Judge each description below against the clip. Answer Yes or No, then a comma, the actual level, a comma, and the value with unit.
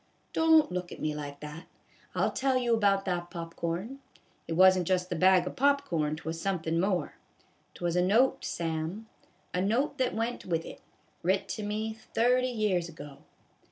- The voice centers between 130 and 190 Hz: Yes, medium, 185 Hz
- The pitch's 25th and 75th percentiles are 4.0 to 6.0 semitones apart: Yes, average, 5.1 semitones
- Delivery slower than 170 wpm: No, average, 185 wpm